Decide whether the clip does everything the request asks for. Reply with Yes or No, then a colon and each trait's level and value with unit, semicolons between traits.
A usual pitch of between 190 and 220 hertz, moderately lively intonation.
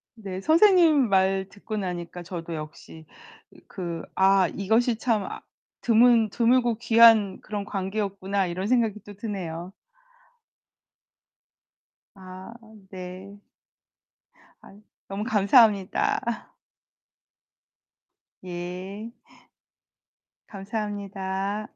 Yes: high, 200 Hz; average, 3.0 semitones